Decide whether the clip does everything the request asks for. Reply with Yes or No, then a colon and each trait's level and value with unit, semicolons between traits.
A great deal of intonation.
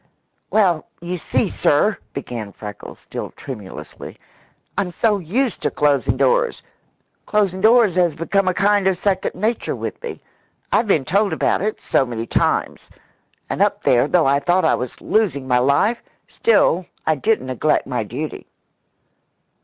Yes: wide, 7.1 semitones